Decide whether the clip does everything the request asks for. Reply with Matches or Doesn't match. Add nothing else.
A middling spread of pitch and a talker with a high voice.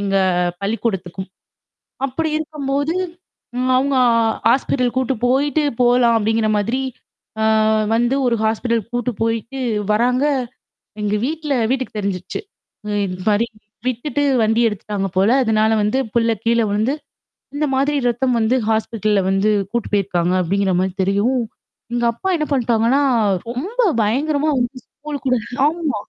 Matches